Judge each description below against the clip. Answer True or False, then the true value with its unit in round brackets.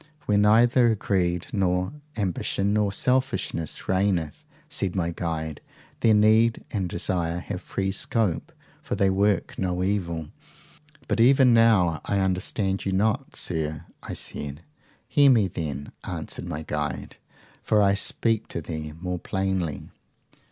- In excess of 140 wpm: False (135 wpm)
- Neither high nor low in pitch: False (95 Hz)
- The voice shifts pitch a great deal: False (3.8 semitones)